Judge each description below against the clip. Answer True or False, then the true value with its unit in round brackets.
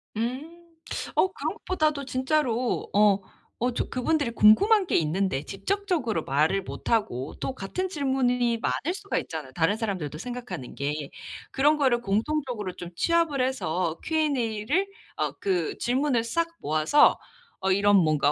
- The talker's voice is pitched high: True (235 Hz)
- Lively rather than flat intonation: True (7.8 semitones)